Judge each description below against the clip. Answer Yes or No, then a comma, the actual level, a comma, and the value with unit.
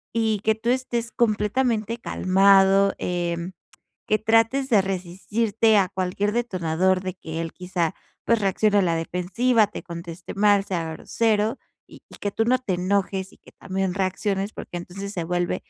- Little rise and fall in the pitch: No, average, 3.3 semitones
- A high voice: Yes, high, 195 Hz